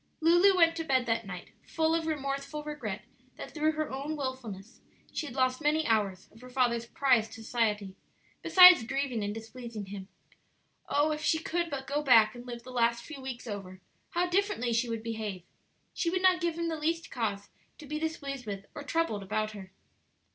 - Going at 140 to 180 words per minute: No, average, 190 wpm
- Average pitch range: No, wide, 5.8 semitones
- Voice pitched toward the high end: Yes, very high, 255 Hz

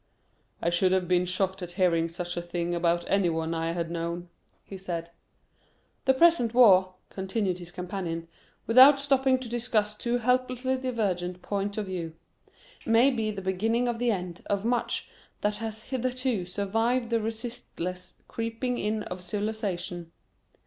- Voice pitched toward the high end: Yes, high, 200 Hz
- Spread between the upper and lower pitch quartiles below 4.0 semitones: No, average, 4.9 semitones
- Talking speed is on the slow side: No, average, 155 wpm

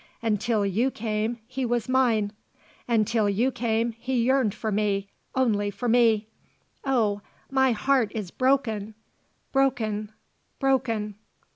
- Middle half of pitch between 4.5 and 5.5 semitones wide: No, average, 3.4 semitones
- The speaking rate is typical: No, slow, 120 wpm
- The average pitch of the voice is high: Yes, high, 225 Hz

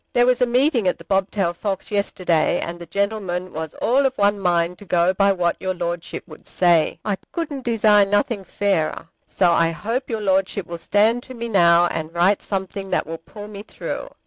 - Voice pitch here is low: No, high, 195 Hz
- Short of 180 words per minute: No, average, 200 wpm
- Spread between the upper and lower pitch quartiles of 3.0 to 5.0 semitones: Yes, average, 3.6 semitones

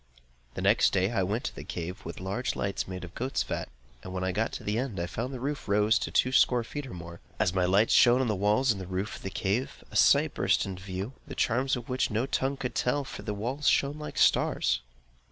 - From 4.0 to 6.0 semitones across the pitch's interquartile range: Yes, average, 5.3 semitones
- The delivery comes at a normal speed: No, fast, 260 wpm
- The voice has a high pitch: No, low, 110 Hz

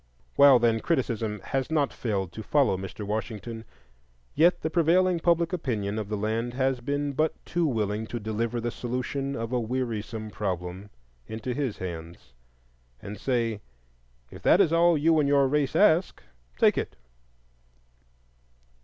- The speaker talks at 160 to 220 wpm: No, average, 150 wpm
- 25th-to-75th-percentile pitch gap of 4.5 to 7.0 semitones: Yes, average, 5.1 semitones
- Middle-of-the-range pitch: No, low, 120 Hz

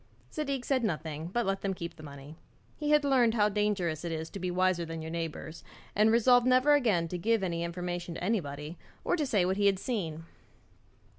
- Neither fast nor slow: No, fast, 210 wpm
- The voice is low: No, medium, 185 Hz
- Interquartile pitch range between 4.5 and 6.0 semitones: Yes, wide, 5.6 semitones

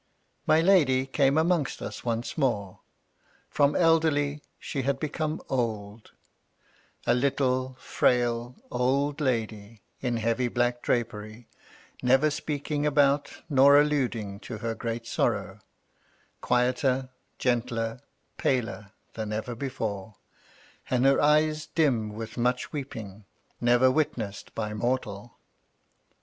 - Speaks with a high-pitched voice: No, low, 125 Hz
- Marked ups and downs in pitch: No, average, 3.8 semitones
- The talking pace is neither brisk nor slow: No, slow, 110 wpm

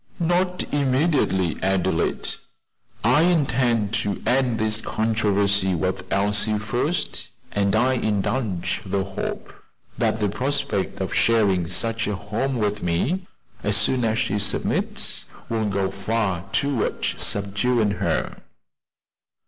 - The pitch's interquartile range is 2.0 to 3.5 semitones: No, average, 4.1 semitones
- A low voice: Yes, low, 105 Hz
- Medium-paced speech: No, slow, 115 wpm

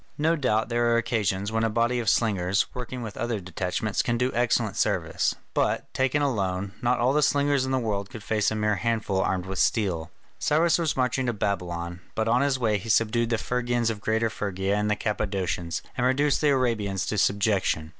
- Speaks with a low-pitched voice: Yes, low, 110 Hz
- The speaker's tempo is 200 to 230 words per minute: Yes, fast, 205 wpm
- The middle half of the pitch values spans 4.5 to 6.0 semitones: No, average, 3.8 semitones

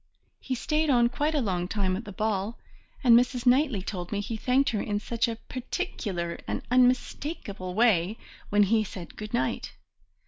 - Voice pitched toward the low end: No, high, 225 Hz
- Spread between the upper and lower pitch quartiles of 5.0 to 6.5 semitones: No, average, 4.0 semitones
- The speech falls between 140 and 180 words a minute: Yes, average, 175 wpm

